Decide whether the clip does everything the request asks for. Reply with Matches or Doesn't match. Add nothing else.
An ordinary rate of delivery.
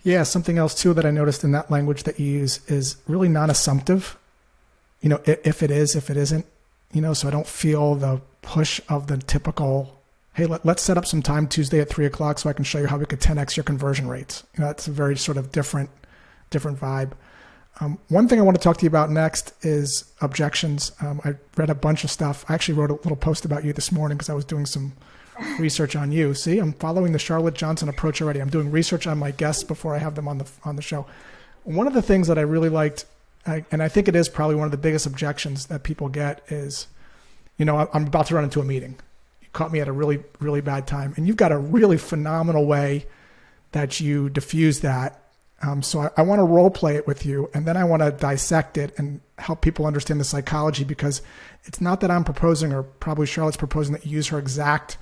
Doesn't match